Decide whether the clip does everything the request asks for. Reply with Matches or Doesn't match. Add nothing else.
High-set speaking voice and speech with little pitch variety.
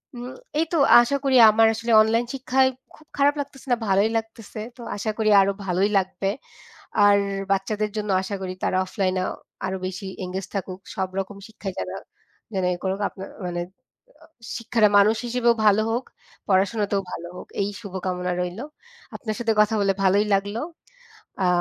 Doesn't match